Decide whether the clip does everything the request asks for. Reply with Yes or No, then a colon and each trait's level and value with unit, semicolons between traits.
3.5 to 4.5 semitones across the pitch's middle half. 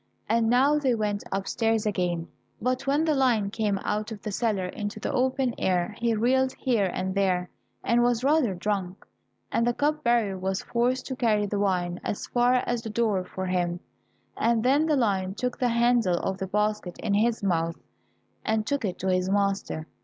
Yes: average, 4.1 semitones